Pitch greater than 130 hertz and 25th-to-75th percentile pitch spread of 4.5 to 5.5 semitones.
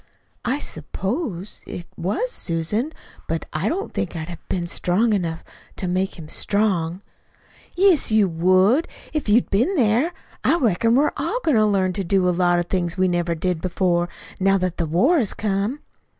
Yes: high, 190 Hz; average, 4.8 semitones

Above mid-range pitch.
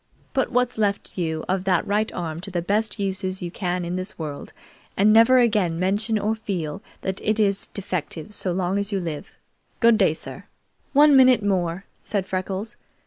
Yes: high, 195 Hz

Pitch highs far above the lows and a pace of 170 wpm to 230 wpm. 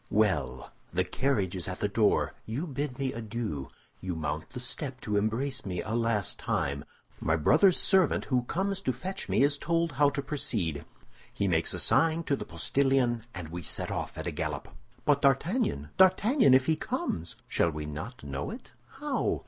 Yes: wide, 8.4 semitones; average, 185 wpm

